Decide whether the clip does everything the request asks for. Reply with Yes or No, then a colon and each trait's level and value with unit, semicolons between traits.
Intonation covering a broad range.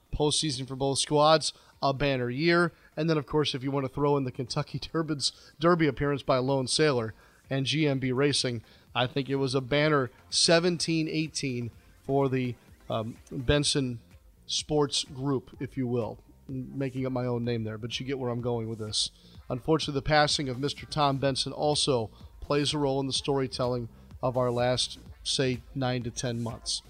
No: average, 3.1 semitones